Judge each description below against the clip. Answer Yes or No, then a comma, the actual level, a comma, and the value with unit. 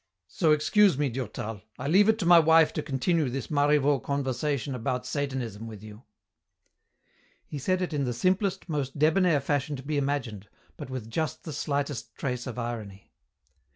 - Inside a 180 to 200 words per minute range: No, average, 170 wpm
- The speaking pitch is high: No, medium, 140 Hz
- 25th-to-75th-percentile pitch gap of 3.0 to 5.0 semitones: Yes, average, 3.9 semitones